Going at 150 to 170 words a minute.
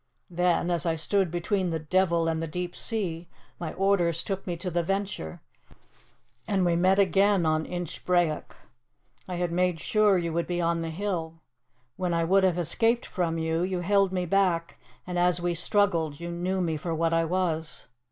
No: average, 185 wpm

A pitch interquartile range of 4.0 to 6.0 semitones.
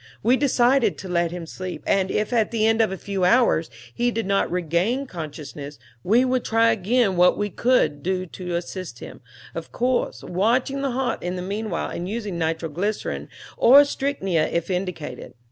Yes: average, 5.2 semitones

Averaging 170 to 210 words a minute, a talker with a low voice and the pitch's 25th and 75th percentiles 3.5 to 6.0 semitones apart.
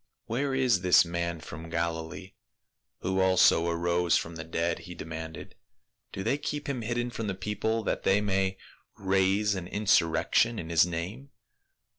Yes: average, 175 wpm; very low, 95 Hz; average, 4.2 semitones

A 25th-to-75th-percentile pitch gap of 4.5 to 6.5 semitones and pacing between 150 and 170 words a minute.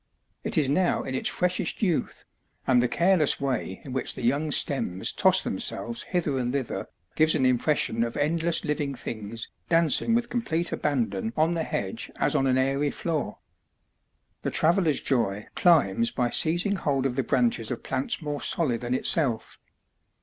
Yes: average, 5.1 semitones; average, 165 wpm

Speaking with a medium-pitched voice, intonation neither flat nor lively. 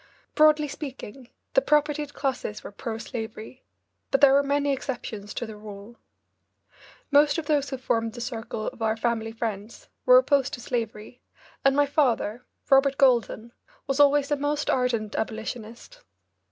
No: very high, 255 Hz; average, 4.2 semitones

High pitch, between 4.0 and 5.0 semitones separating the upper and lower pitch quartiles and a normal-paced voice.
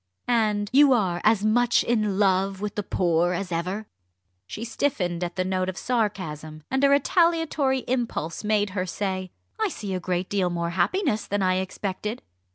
Yes: high, 200 Hz; average, 4.4 semitones; average, 170 wpm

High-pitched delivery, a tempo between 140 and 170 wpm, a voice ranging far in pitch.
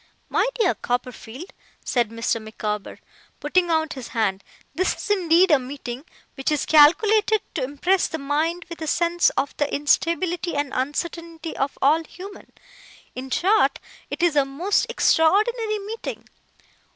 No: very high, 320 Hz; average, 145 wpm; average, 5.0 semitones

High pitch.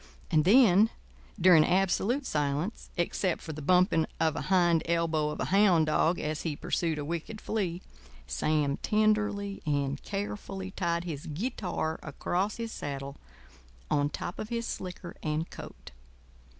No: medium, 170 Hz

